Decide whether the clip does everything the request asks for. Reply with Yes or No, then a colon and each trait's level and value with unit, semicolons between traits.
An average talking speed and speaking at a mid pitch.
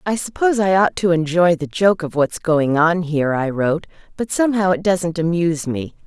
No: fast, 210 wpm; medium, 175 Hz